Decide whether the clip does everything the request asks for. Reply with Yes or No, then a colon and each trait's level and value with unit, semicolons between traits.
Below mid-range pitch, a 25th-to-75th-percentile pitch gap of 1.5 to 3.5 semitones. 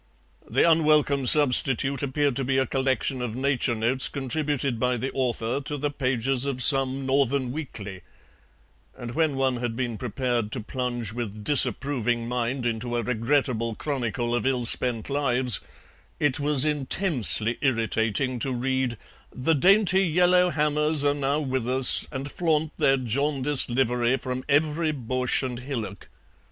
Yes: low, 130 Hz; average, 3.0 semitones